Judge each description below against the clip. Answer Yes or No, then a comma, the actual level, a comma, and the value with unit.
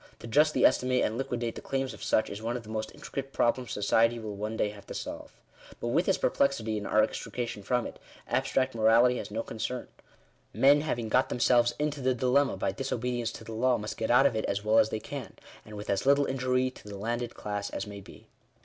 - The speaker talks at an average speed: No, fast, 230 wpm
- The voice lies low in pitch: Yes, low, 120 Hz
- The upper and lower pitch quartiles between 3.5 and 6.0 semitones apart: No, average, 2.9 semitones